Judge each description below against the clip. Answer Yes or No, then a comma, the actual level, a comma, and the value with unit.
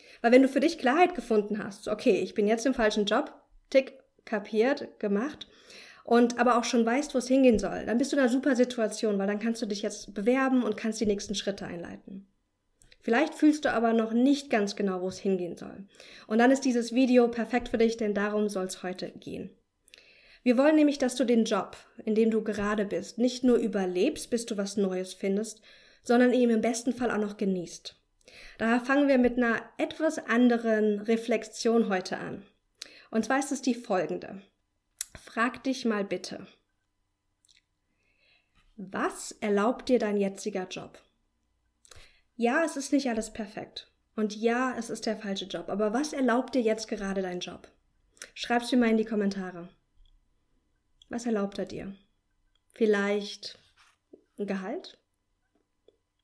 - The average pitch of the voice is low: No, high, 225 Hz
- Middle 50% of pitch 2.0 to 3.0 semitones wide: No, average, 3.4 semitones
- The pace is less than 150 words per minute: No, average, 170 wpm